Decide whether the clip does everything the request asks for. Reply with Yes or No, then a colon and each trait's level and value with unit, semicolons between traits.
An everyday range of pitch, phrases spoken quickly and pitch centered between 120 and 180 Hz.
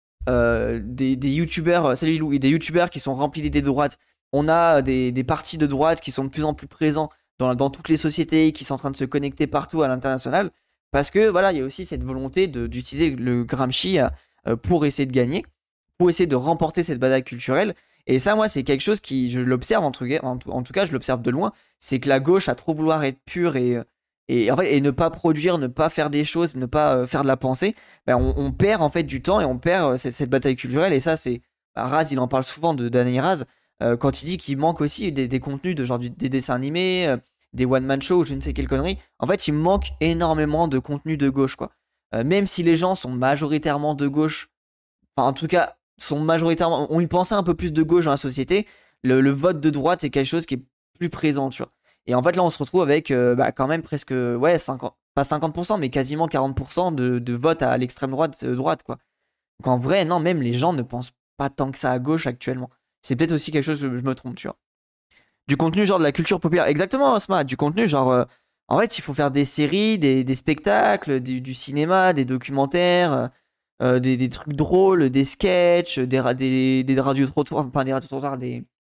Yes: average, 4.0 semitones; fast, 235 wpm; medium, 140 Hz